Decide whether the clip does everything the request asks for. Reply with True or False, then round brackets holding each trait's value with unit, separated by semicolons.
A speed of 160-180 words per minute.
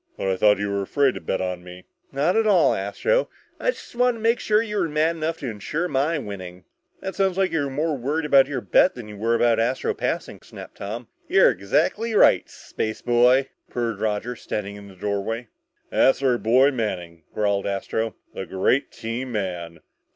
False (190 wpm)